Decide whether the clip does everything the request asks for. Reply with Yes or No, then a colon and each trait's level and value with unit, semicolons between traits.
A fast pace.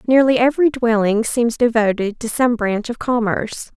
No: average, 160 wpm